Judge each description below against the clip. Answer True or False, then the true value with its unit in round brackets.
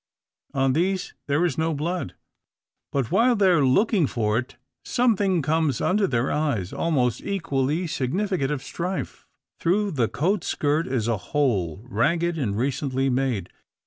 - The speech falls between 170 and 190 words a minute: False (145 wpm)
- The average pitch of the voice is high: False (145 Hz)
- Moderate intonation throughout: False (5.8 semitones)